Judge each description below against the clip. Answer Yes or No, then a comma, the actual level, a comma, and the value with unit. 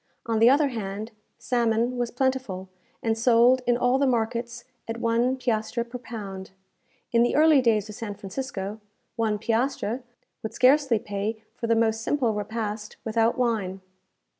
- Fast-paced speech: No, average, 155 wpm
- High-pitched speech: Yes, high, 230 Hz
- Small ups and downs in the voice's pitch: Yes, narrow, 2.2 semitones